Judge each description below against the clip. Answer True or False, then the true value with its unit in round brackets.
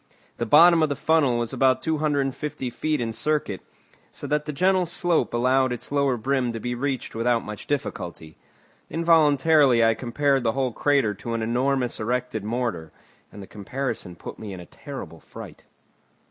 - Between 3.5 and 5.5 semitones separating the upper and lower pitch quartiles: True (4.1 semitones)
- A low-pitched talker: True (130 Hz)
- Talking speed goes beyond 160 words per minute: True (170 wpm)